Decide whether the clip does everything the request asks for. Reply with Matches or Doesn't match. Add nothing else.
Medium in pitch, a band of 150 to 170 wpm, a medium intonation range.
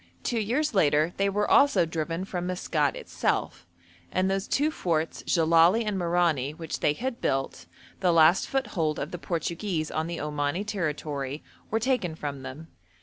Matches